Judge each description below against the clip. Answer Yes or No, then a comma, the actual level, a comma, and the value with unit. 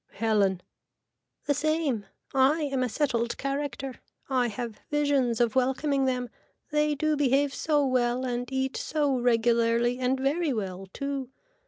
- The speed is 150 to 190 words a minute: No, average, 140 wpm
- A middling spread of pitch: Yes, average, 3.0 semitones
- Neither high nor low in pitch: No, very high, 260 Hz